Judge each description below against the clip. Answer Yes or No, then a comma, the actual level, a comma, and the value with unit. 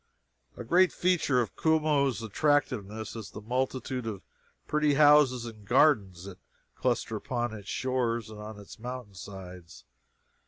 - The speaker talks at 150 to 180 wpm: No, average, 140 wpm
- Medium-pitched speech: No, low, 120 Hz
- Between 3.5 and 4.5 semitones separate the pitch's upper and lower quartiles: No, average, 5.1 semitones